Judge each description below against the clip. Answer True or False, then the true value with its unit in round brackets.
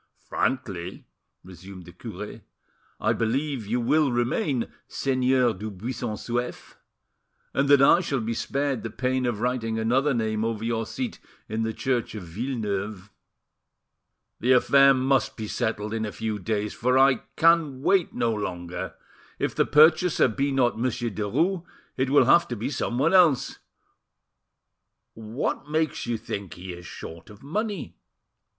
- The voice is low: True (120 Hz)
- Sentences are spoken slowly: False (150 wpm)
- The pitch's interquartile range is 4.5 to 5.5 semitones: False (4.1 semitones)